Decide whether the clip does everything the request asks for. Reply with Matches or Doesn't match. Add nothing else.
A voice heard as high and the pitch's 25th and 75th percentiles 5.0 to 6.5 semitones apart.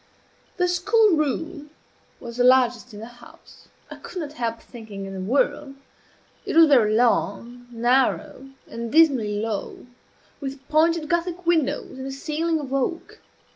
Matches